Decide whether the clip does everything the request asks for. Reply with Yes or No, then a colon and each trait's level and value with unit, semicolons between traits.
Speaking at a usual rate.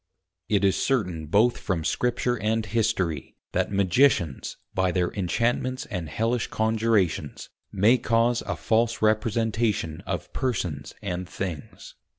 No: slow, 125 wpm